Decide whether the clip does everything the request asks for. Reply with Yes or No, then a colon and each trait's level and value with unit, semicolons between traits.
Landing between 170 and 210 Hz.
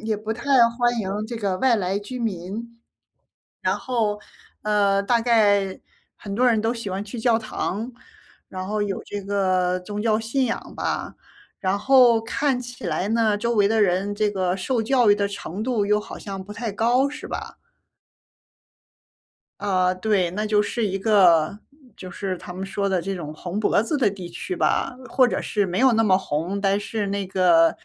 Yes: high, 205 Hz